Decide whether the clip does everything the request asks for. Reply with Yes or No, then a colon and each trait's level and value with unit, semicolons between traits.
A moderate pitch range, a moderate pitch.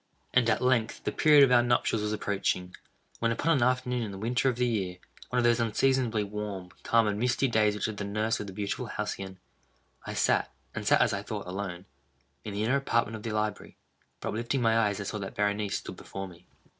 No: average, 3.0 semitones; low, 110 Hz